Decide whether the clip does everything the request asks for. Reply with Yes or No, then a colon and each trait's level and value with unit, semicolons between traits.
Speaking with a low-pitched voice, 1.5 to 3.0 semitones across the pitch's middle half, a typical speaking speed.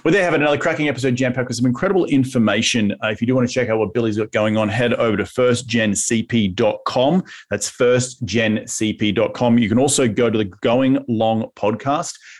Yes: low, 120 Hz; narrow, 2.6 semitones; average, 195 wpm